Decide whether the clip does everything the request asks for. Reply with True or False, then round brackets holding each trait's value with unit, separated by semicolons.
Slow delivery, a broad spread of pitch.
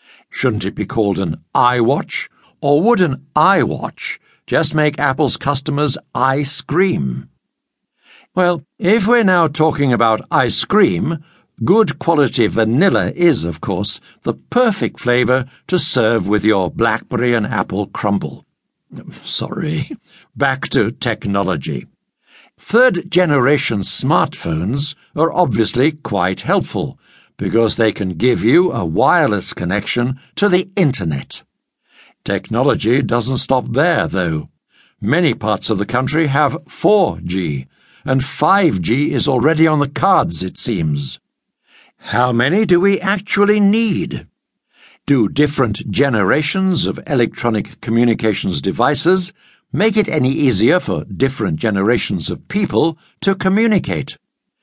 True (120 wpm; 7.4 semitones)